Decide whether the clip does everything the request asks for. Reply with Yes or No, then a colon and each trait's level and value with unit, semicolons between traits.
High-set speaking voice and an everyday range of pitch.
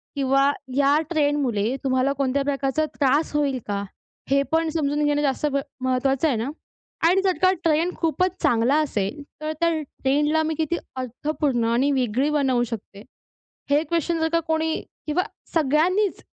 Yes: very high, 285 Hz; average, 3.2 semitones